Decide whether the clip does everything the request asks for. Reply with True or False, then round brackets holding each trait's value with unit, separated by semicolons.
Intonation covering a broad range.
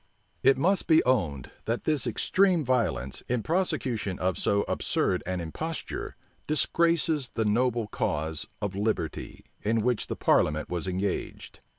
True (8.3 semitones)